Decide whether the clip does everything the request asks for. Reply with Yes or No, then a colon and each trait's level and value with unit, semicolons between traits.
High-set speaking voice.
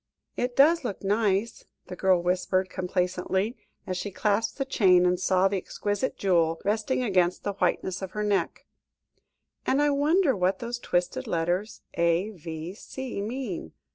Yes: high, 195 Hz